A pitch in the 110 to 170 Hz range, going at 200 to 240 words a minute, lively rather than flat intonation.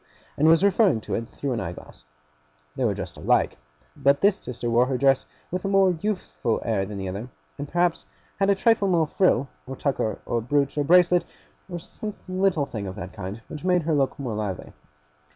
Yes: medium, 140 Hz; fast, 205 wpm; wide, 7.6 semitones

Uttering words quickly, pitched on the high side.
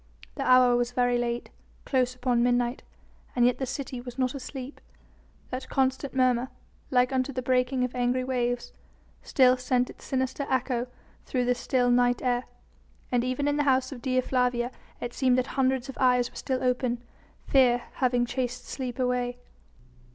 No: average, 170 wpm; very high, 250 Hz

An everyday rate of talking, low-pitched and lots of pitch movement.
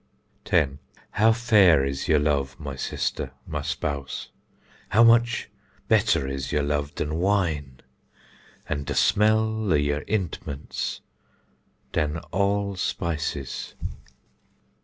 No: slow, 110 wpm; very low, 80 Hz; wide, 6.3 semitones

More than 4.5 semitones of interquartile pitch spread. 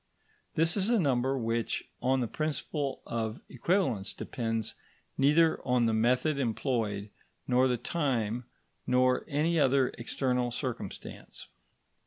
No: average, 3.7 semitones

